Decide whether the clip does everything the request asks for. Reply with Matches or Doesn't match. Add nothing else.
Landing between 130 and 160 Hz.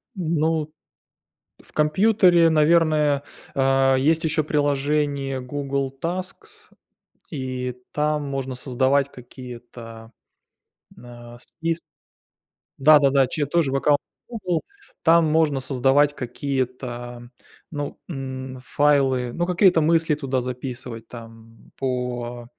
Matches